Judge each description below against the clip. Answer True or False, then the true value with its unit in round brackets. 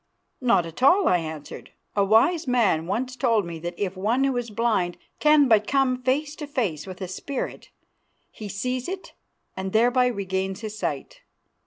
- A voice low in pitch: False (230 Hz)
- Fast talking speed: False (175 wpm)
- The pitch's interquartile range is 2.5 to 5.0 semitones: False (5.4 semitones)